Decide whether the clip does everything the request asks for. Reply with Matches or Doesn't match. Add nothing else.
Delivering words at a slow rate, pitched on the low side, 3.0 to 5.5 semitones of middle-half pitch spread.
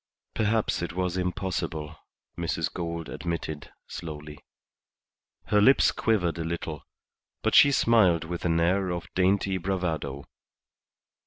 Doesn't match